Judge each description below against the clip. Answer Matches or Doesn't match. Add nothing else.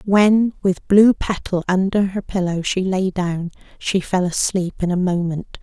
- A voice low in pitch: Doesn't match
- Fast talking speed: Doesn't match